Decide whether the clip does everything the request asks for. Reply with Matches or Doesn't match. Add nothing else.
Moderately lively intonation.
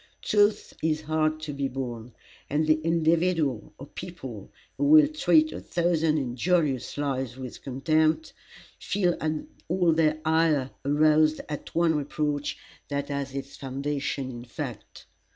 Matches